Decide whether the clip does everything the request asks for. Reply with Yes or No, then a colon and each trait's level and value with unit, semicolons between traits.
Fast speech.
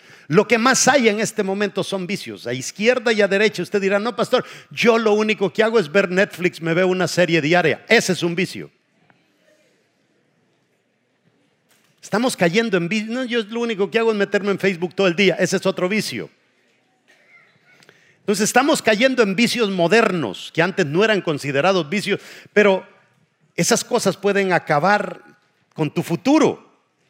No: average, 170 wpm